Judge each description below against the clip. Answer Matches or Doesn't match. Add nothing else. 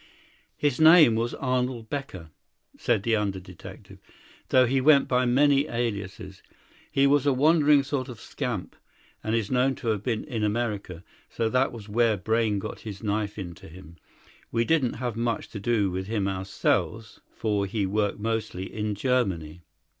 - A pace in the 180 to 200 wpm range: Doesn't match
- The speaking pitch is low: Matches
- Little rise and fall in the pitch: Doesn't match